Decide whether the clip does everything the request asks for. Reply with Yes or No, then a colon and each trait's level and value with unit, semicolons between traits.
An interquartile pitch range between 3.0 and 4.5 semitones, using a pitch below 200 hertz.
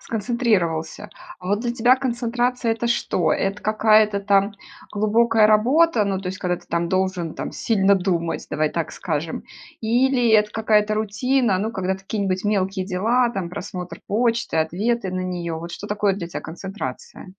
No: average, 3.7 semitones; high, 205 Hz